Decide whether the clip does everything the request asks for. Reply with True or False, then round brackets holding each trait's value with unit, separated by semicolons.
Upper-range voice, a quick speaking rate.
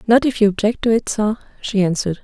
True (215 Hz; 240 wpm)